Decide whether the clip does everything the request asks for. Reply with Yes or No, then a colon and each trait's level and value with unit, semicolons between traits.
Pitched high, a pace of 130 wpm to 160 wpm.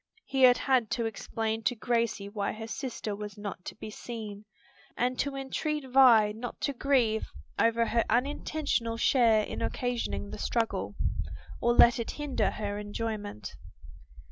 Yes: high, 230 Hz; average, 150 wpm